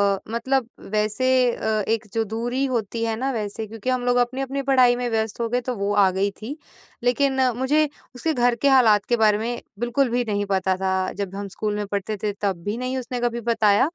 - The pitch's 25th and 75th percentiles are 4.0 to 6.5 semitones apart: No, average, 3.2 semitones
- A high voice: Yes, high, 230 Hz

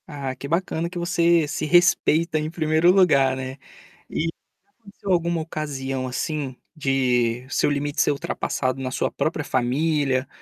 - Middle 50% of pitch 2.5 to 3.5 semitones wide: No, average, 3.9 semitones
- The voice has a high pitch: No, medium, 150 Hz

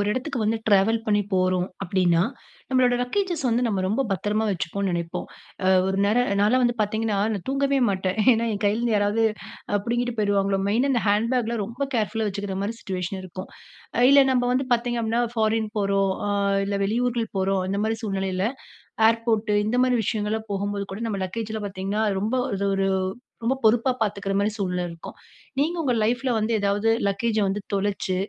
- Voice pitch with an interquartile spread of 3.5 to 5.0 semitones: No, average, 3.1 semitones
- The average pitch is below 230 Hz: Yes, high, 210 Hz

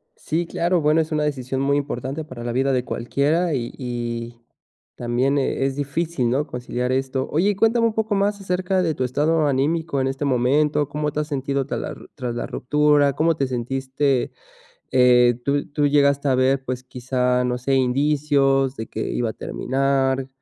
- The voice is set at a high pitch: No, medium, 140 Hz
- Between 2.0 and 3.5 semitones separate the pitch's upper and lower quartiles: Yes, average, 2.8 semitones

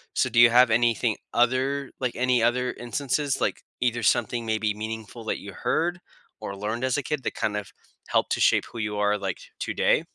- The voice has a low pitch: Yes, low, 120 Hz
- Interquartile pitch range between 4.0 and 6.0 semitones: No, average, 2.7 semitones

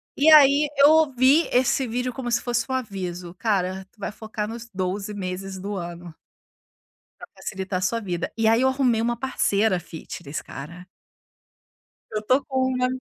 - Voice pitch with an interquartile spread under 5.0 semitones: No, wide, 5.6 semitones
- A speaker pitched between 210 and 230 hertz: Yes, high, 220 Hz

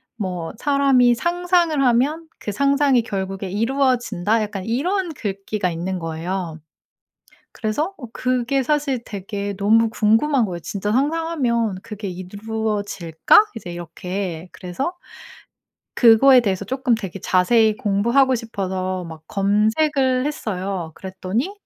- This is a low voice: No, high, 220 Hz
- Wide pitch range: Yes, wide, 5.7 semitones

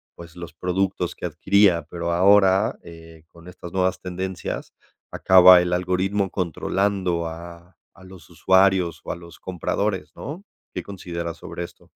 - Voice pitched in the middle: No, very low, 90 Hz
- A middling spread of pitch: No, narrow, 1.8 semitones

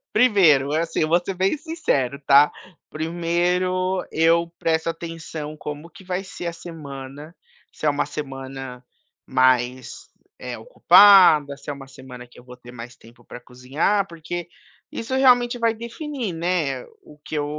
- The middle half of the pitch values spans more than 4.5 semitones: Yes, average, 5.2 semitones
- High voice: No, medium, 160 Hz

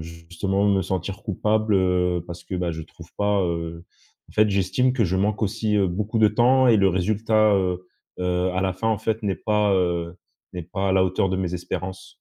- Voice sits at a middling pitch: No, very low, 95 Hz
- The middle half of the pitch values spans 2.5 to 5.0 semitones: Yes, average, 2.9 semitones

